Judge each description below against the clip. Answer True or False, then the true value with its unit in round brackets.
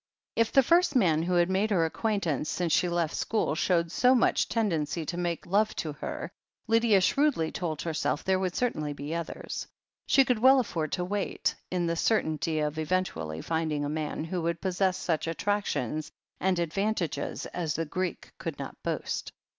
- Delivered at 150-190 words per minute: True (180 wpm)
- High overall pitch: False (175 Hz)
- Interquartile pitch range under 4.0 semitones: False (4.4 semitones)